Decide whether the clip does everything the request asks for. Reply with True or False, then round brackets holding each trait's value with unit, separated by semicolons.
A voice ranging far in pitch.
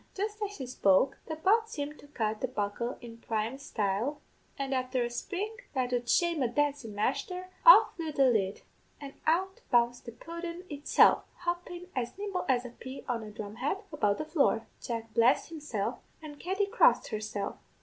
True (6.5 semitones)